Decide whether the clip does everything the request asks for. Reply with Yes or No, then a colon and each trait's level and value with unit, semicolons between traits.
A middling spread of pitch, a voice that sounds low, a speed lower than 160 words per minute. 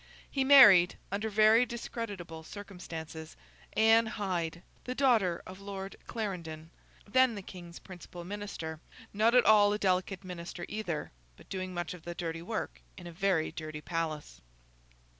No: average, 4.0 semitones; medium, 185 Hz; average, 140 wpm